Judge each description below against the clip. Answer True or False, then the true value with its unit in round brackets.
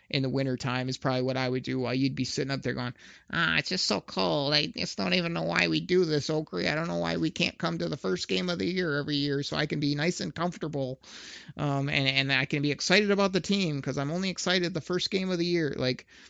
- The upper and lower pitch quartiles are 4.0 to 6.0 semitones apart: True (4.9 semitones)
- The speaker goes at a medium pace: False (275 wpm)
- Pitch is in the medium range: True (145 Hz)